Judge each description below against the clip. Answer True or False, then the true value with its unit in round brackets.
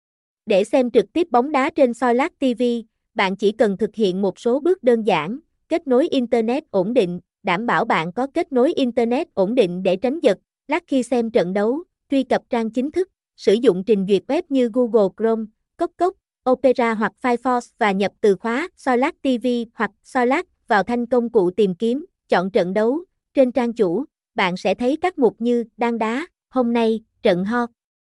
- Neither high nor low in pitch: False (240 Hz)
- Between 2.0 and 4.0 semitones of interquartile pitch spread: True (3.5 semitones)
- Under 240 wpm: True (195 wpm)